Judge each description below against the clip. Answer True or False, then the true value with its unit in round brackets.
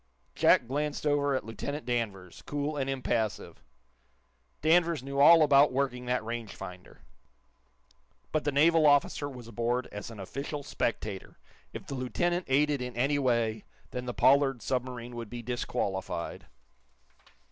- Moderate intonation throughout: True (3.5 semitones)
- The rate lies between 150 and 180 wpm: False (140 wpm)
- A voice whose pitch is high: False (130 Hz)